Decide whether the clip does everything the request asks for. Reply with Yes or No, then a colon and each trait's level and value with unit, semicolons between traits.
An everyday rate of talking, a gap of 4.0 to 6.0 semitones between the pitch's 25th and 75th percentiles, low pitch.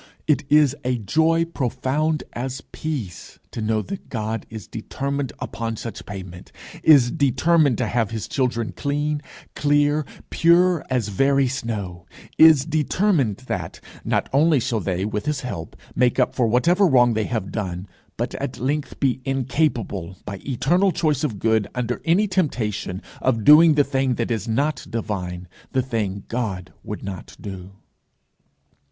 Yes: average, 150 wpm; wide, 5.5 semitones; low, 125 Hz